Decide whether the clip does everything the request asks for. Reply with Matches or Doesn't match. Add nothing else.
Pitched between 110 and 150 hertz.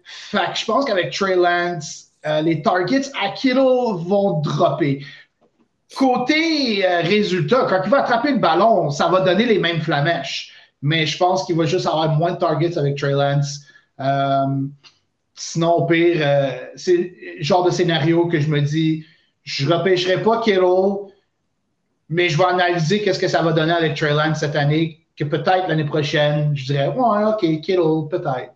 Doesn't match